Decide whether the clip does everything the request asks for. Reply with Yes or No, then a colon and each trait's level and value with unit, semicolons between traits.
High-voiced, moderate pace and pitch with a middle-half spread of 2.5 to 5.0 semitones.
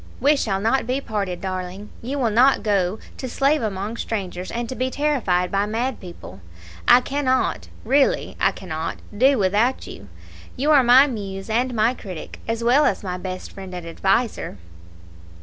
No: high, 220 Hz; average, 170 wpm; wide, 5.4 semitones